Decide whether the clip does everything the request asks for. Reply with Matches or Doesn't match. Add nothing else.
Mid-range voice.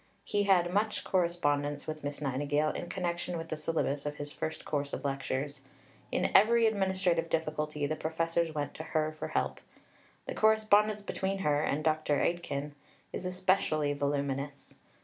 Matches